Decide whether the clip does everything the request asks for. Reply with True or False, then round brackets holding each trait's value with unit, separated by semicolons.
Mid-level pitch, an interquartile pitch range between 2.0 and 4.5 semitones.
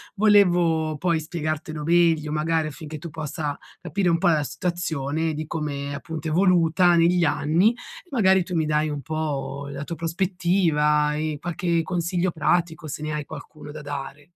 True (160 Hz; 2.5 semitones)